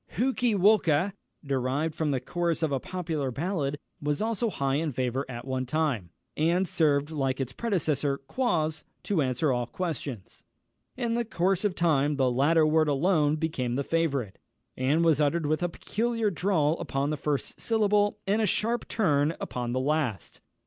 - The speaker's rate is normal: Yes, average, 170 wpm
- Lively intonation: No, average, 4.8 semitones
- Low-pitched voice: No, medium, 155 Hz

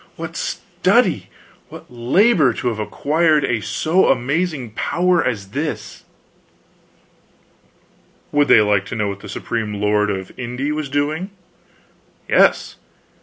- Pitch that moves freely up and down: Yes, wide, 6.4 semitones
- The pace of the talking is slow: Yes, slow, 120 wpm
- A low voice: Yes, low, 125 Hz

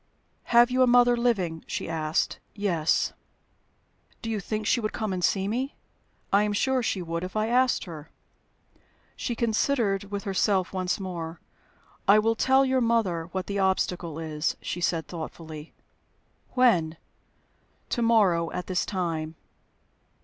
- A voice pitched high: Yes, high, 195 Hz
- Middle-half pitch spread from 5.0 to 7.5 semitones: Yes, wide, 5.4 semitones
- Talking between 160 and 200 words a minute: No, average, 150 wpm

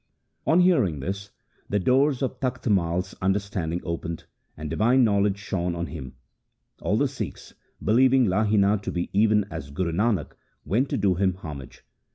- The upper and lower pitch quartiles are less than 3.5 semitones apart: No, average, 4.5 semitones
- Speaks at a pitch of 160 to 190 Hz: No, low, 100 Hz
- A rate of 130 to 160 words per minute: No, average, 170 wpm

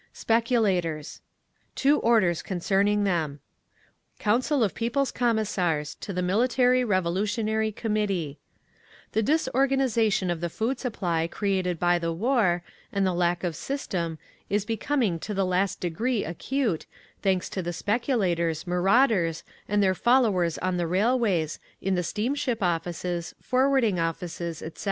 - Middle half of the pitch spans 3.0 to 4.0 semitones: No, average, 5.0 semitones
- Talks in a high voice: Yes, high, 195 Hz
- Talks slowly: Yes, slow, 130 wpm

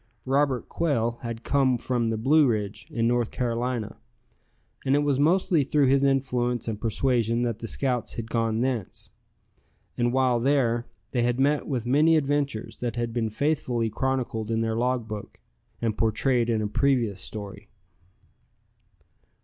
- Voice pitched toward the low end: Yes, low, 120 Hz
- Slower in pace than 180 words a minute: Yes, average, 155 wpm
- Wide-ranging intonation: No, average, 3.0 semitones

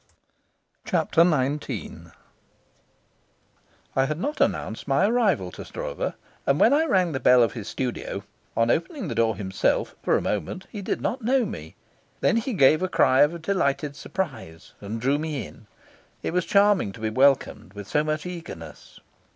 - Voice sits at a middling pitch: Yes, medium, 145 Hz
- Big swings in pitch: Yes, wide, 8.3 semitones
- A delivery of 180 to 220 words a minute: No, average, 165 wpm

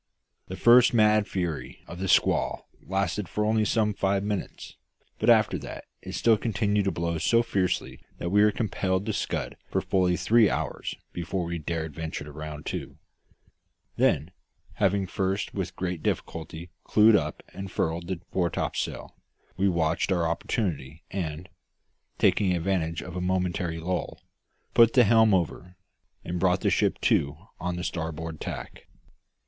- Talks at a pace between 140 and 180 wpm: Yes, average, 155 wpm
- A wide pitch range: No, average, 3.4 semitones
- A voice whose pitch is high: No, very low, 90 Hz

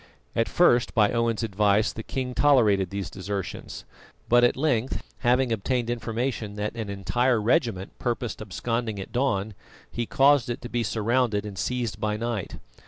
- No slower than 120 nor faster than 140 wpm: No, average, 160 wpm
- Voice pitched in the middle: No, low, 115 Hz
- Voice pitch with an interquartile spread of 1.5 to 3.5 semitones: Yes, average, 2.8 semitones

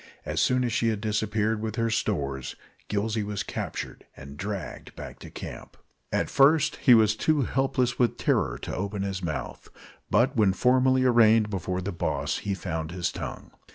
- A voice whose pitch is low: Yes, low, 105 Hz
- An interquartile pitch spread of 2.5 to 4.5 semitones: Yes, average, 3.8 semitones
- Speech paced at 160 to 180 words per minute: Yes, average, 175 wpm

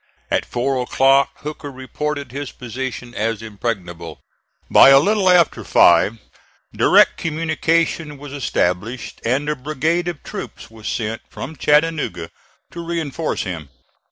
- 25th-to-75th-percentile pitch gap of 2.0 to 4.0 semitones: No, average, 5.3 semitones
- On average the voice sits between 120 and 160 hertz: Yes, low, 135 Hz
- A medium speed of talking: No, slow, 130 wpm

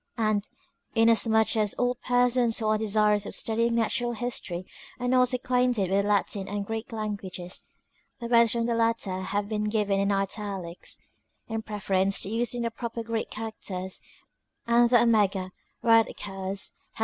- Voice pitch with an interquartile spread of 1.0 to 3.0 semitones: Yes, average, 2.7 semitones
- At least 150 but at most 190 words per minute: Yes, average, 170 wpm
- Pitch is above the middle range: Yes, high, 220 Hz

